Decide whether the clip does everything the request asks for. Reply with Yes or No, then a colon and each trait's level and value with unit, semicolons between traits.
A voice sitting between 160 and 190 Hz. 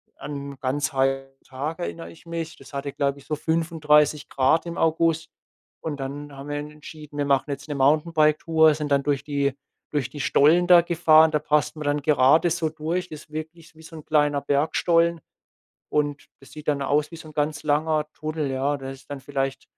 No: medium, 150 Hz